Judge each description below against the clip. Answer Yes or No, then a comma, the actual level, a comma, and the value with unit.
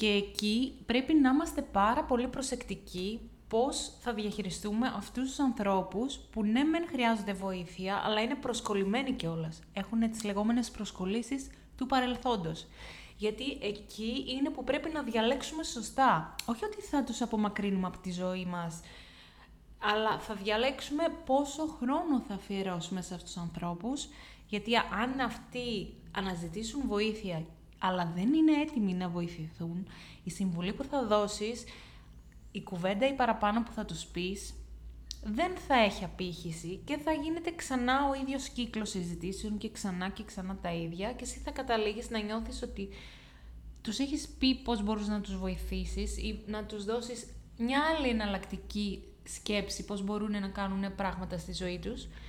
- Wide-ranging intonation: No, average, 4.9 semitones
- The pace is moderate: Yes, average, 150 wpm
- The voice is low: No, high, 215 Hz